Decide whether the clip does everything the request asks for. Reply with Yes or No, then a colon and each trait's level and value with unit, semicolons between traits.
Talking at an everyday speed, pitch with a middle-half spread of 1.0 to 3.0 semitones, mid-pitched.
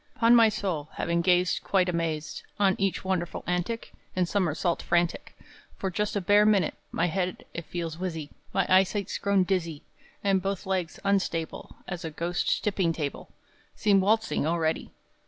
Yes: average, 155 wpm; average, 2.7 semitones; medium, 180 Hz